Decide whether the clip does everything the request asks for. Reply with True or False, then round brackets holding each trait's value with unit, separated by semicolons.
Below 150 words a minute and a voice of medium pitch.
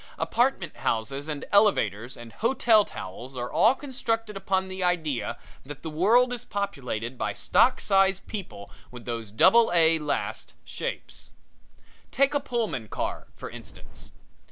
True (140 wpm; 180 Hz)